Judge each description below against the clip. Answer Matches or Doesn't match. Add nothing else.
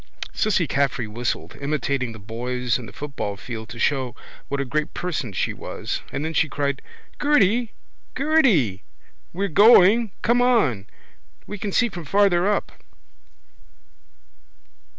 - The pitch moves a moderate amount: Doesn't match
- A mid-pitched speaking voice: Matches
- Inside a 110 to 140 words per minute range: Matches